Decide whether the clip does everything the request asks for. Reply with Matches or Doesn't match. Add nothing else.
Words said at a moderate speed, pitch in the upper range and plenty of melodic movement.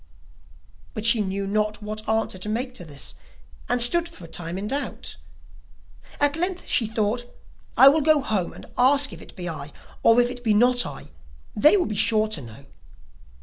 Doesn't match